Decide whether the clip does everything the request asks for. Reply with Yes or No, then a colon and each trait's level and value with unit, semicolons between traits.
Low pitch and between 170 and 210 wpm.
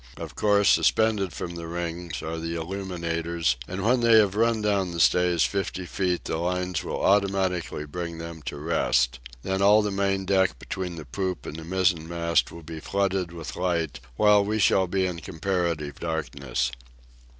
Yes: very low, 90 Hz; average, 175 wpm